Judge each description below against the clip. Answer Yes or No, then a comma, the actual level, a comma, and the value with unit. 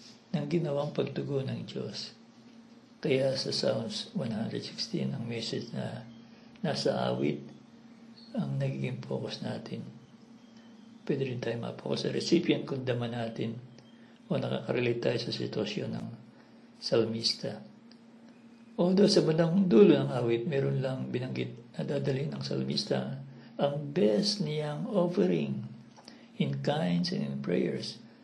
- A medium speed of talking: Yes, average, 120 wpm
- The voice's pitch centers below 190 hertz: Yes, medium, 140 Hz